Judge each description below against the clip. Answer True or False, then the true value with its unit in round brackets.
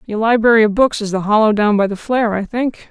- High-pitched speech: True (220 Hz)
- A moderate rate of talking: False (270 wpm)